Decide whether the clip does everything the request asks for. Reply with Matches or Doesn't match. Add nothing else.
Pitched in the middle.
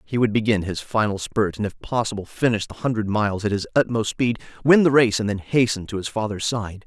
Doesn't match